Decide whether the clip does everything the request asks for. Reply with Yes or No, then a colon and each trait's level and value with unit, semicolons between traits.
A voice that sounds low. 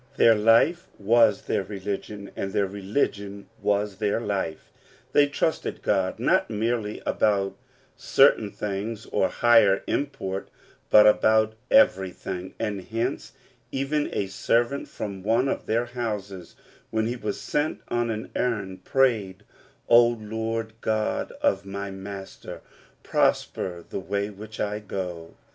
Yes: low, 105 Hz